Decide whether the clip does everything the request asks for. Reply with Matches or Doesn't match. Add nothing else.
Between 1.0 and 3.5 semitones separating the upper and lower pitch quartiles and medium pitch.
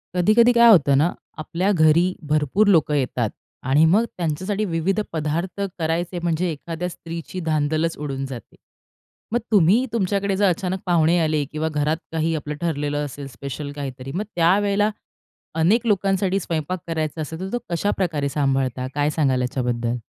Doesn't match